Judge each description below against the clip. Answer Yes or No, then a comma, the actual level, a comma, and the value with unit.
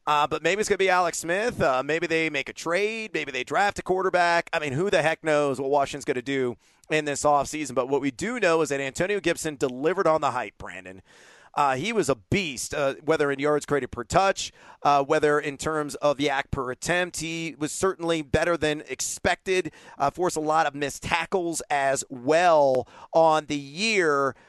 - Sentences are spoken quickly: Yes, fast, 210 wpm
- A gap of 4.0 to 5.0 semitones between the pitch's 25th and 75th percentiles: No, average, 3.3 semitones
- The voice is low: No, medium, 150 Hz